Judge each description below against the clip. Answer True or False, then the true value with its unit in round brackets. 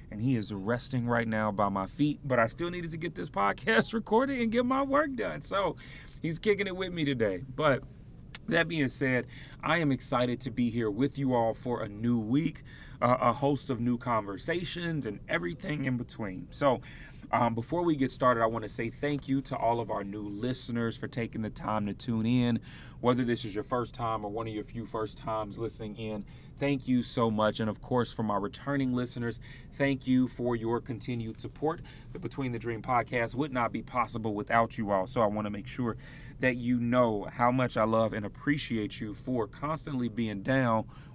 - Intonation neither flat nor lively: True (3.6 semitones)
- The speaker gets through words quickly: True (210 wpm)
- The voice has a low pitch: True (120 Hz)